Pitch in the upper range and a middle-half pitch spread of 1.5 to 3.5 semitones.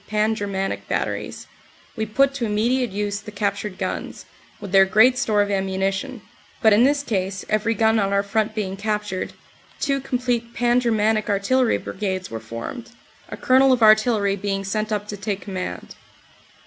Yes: high, 210 Hz; average, 3.0 semitones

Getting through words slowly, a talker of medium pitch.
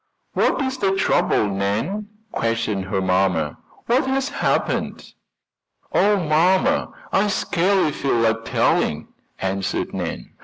Yes: slow, 115 wpm; medium, 150 Hz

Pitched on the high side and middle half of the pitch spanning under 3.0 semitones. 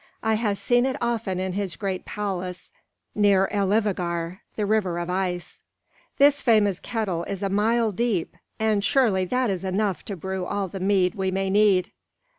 Yes: high, 200 Hz; narrow, 2.6 semitones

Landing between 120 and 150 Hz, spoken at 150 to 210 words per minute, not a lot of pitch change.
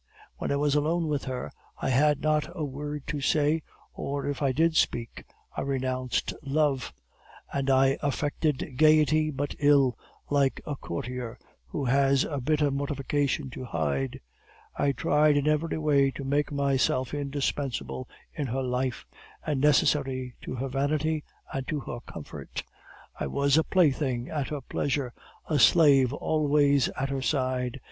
Yes: medium, 140 Hz; average, 155 wpm; narrow, 2.2 semitones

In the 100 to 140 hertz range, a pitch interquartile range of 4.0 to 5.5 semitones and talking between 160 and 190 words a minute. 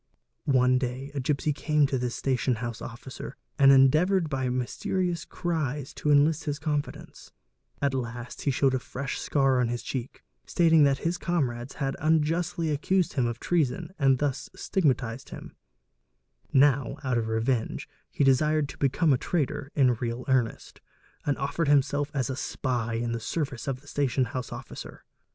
No: low, 135 Hz; average, 3.0 semitones; average, 170 wpm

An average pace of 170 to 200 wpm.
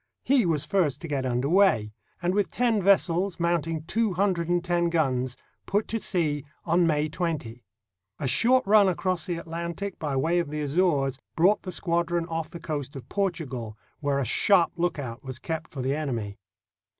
Yes: average, 185 wpm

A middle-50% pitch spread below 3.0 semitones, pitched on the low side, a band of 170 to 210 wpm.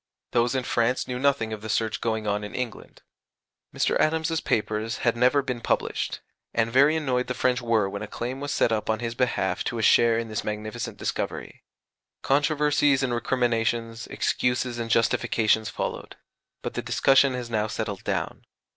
Yes: narrow, 2.6 semitones; low, 120 Hz; average, 175 wpm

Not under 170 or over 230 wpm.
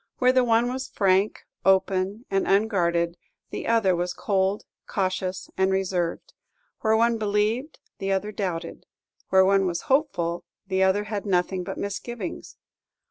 No: average, 140 wpm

